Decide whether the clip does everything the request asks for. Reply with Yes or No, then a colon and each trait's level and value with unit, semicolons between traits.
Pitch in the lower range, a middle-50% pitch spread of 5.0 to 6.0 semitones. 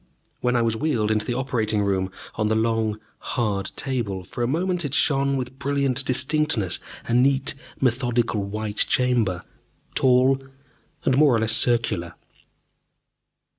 No: low, 120 Hz; average, 3.7 semitones